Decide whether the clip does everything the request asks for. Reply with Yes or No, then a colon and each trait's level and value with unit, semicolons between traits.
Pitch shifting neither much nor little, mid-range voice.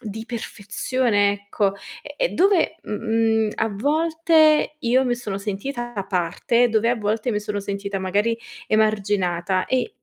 No: average, 3.4 semitones; high, 220 Hz